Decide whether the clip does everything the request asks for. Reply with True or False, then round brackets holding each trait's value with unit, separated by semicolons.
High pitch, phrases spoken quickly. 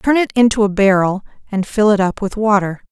True (205 Hz; 225 wpm)